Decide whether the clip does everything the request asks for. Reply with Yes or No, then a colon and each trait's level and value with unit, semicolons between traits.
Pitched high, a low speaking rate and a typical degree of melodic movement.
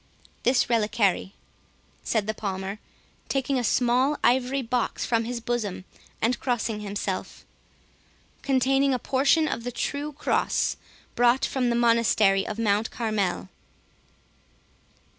Yes: high, 235 Hz; slow, 120 wpm; average, 3.4 semitones